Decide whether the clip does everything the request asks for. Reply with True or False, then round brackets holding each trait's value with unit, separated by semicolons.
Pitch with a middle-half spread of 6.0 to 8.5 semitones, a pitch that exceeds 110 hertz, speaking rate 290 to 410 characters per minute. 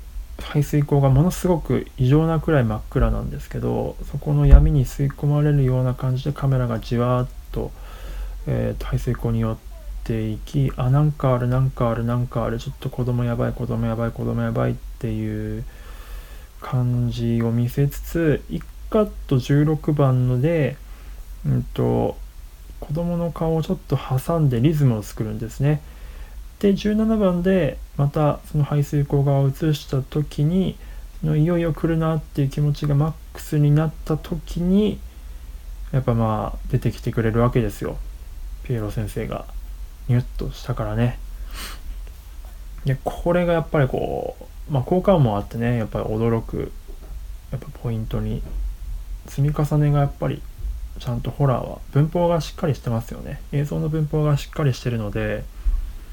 False (5.2 semitones; 130 Hz; 315 characters per minute)